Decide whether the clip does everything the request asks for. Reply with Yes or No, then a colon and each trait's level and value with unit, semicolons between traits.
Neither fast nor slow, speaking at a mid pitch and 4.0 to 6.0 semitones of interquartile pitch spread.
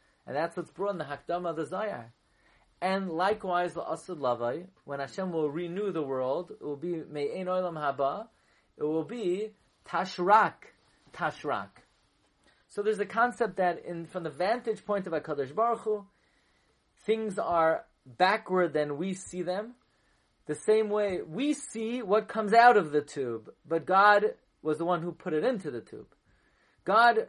Yes: average, 165 wpm; medium, 180 Hz; average, 5.1 semitones